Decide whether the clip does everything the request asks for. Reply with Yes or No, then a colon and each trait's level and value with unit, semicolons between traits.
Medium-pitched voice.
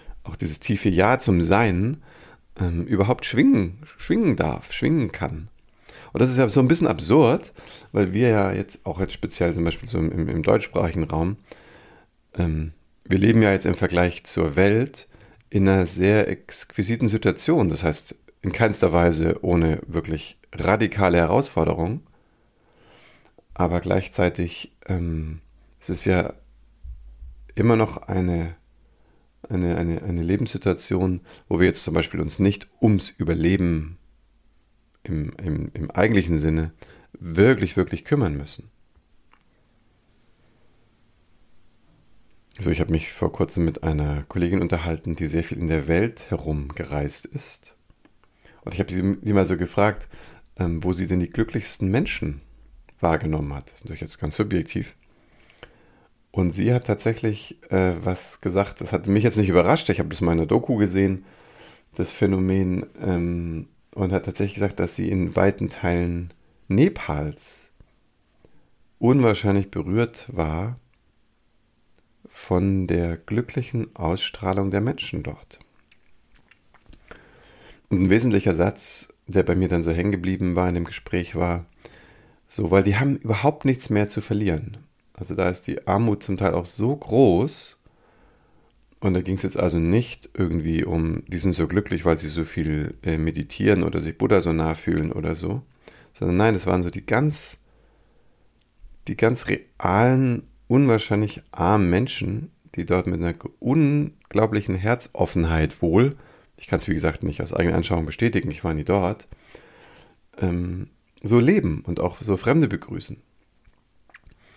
No: very low, 95 Hz